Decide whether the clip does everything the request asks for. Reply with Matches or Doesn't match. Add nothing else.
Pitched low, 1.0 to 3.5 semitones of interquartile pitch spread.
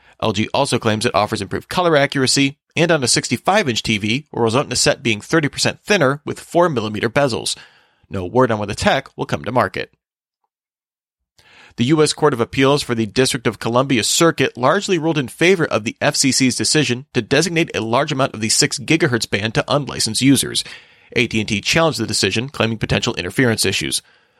Doesn't match